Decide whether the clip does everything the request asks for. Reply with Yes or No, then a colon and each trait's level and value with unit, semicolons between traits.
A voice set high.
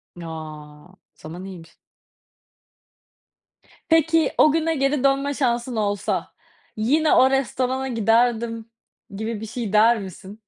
Yes: high, 230 Hz